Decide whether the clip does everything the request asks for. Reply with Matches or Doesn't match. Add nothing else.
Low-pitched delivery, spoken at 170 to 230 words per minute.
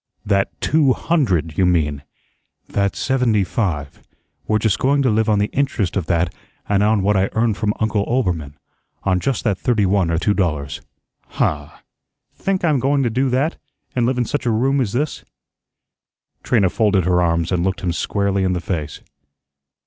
Matches